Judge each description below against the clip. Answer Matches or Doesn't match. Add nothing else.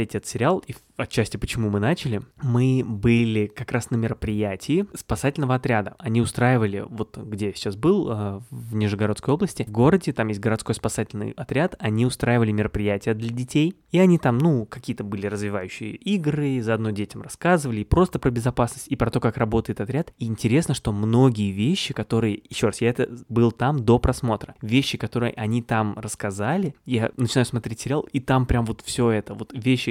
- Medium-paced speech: Doesn't match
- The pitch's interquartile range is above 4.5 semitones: Doesn't match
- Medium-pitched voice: Doesn't match